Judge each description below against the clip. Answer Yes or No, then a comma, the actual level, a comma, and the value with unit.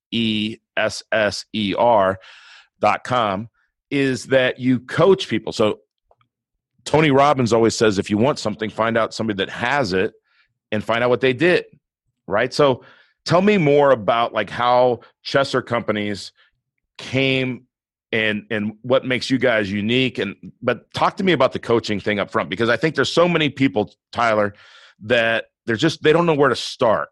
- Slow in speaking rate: No, average, 175 wpm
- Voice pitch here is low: Yes, low, 120 Hz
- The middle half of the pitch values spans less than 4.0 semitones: Yes, average, 3.6 semitones